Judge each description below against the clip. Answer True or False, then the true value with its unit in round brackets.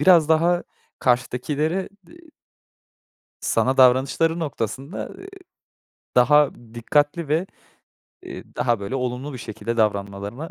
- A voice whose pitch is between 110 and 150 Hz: True (135 Hz)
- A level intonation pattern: False (4.9 semitones)